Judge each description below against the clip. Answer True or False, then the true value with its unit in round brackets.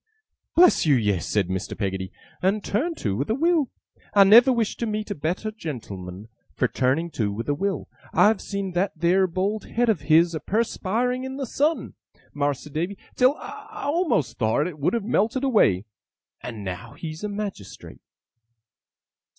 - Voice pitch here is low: False (190 Hz)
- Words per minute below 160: False (170 wpm)